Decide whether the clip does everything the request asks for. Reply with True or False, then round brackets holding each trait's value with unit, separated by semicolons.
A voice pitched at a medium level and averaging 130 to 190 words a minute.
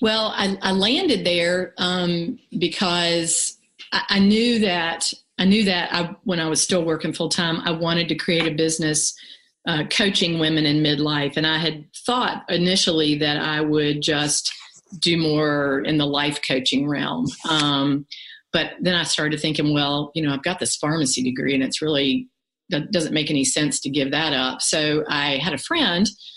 True (160 Hz; 180 wpm)